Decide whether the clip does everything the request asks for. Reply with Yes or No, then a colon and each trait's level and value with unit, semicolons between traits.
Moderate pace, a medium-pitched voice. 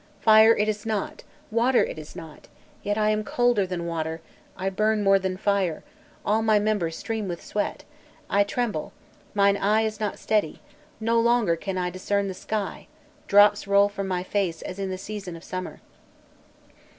No: average, 175 wpm; high, 200 Hz